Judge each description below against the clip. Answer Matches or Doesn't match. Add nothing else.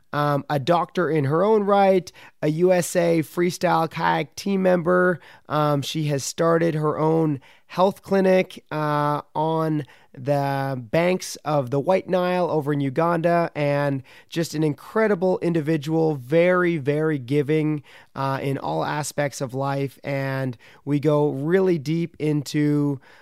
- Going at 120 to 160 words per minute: Matches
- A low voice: Doesn't match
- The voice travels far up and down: Doesn't match